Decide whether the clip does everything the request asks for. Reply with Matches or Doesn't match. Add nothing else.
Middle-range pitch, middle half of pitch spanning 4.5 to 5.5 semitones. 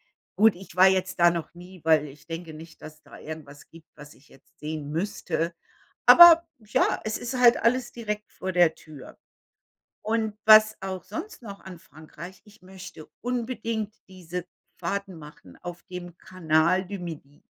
Matches